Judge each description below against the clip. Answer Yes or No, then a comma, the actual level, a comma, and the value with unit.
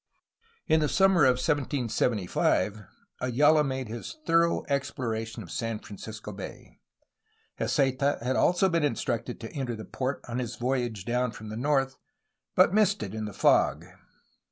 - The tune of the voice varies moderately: Yes, average, 4.4 semitones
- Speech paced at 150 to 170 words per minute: Yes, average, 155 wpm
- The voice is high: No, low, 125 Hz